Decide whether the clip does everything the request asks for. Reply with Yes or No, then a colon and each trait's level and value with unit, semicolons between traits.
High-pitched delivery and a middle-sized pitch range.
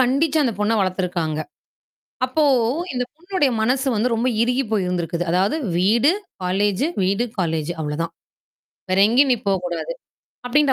No: high, 210 Hz; wide, 6.0 semitones